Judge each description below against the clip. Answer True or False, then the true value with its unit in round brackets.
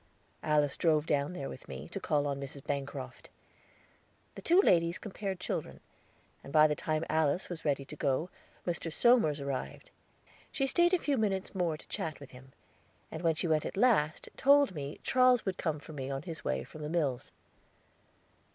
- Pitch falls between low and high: True (155 Hz)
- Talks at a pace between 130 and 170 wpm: False (185 wpm)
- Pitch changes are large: False (4.8 semitones)